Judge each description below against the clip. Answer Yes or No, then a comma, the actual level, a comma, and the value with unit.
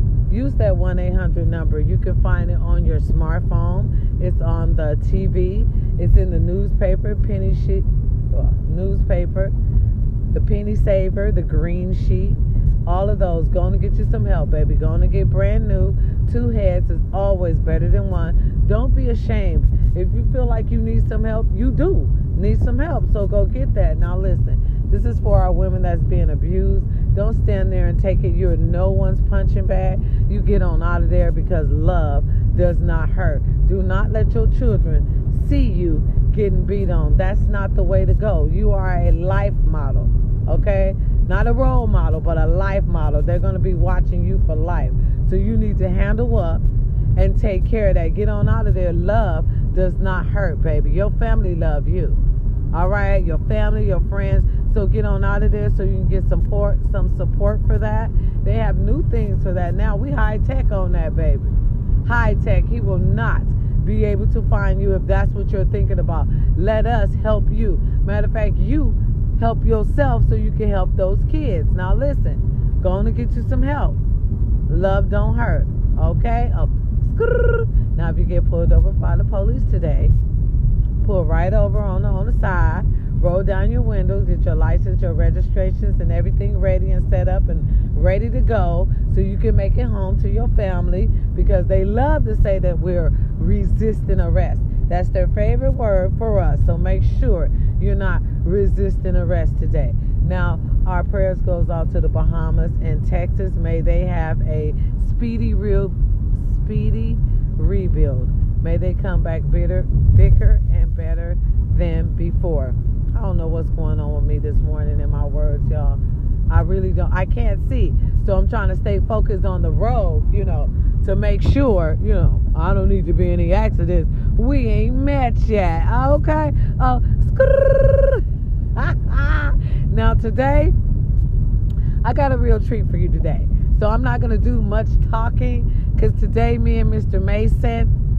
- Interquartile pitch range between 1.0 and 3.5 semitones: Yes, average, 2.7 semitones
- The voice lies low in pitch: Yes, low, 105 Hz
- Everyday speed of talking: Yes, average, 180 wpm